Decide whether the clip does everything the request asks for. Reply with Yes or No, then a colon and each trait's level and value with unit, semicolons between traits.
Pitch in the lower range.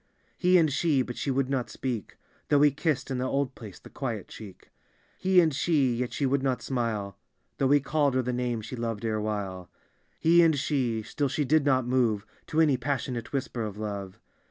Yes: low, 130 Hz